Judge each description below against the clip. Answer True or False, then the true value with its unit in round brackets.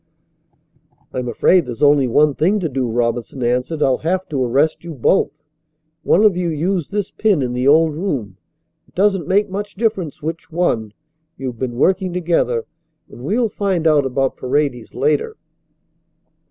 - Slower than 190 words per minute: True (160 wpm)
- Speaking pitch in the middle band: True (150 Hz)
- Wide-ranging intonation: True (6.4 semitones)